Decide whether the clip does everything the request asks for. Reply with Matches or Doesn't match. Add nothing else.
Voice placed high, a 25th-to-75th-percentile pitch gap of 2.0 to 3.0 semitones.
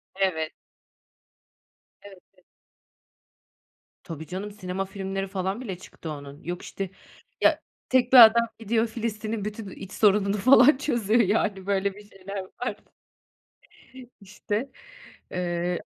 Matches